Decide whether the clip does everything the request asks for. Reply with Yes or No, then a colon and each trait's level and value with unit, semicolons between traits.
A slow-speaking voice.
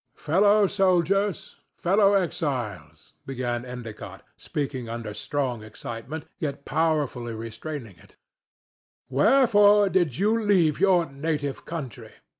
Yes: slow, 100 wpm